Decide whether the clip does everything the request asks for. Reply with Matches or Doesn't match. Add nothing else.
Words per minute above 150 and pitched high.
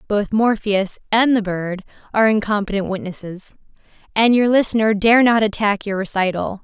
Doesn't match